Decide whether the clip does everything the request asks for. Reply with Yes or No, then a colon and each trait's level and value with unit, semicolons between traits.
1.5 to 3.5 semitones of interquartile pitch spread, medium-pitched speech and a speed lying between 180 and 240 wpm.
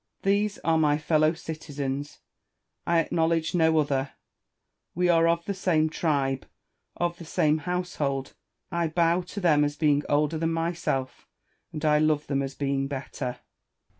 No: average, 2.7 semitones; medium, 155 Hz; average, 150 wpm